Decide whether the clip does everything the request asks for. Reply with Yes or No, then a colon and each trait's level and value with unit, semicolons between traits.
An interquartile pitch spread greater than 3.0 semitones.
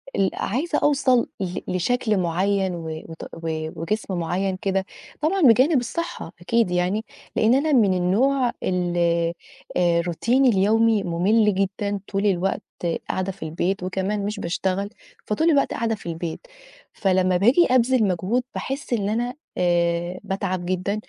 Yes: average, 4.4 semitones